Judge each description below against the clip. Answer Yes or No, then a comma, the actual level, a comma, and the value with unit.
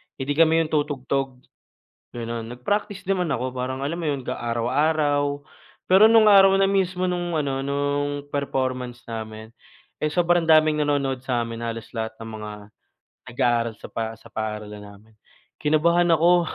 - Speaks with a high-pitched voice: No, medium, 140 Hz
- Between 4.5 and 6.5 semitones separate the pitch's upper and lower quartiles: Yes, wide, 5.6 semitones